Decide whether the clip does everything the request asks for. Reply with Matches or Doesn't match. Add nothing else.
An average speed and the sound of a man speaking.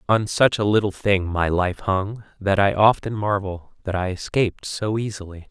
Matches